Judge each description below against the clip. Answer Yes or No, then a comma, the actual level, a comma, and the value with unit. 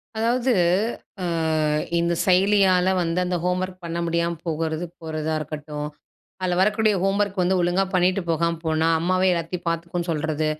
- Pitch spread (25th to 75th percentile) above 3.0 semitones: No, narrow, 2.4 semitones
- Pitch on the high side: No, medium, 175 Hz